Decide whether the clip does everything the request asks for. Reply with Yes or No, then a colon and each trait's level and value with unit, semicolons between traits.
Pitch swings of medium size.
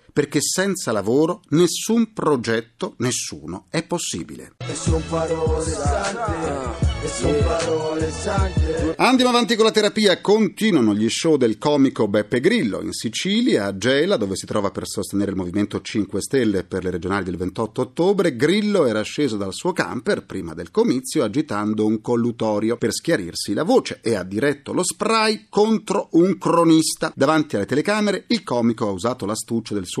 No: wide, 8.3 semitones